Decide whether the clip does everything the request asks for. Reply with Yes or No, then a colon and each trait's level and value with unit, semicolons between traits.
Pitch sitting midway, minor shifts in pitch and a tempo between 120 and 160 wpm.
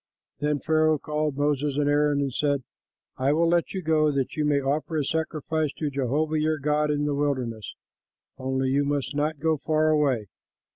No: medium, 150 Hz; narrow, 1.8 semitones; average, 190 wpm